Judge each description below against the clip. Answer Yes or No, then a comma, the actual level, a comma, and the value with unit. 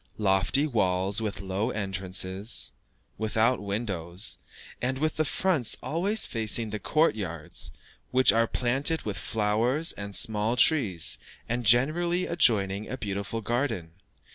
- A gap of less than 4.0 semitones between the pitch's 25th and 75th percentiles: No, average, 4.8 semitones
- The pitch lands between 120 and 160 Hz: No, low, 110 Hz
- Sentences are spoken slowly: Yes, slow, 125 wpm